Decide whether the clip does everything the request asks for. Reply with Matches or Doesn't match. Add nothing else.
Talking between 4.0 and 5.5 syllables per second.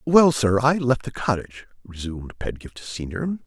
Matches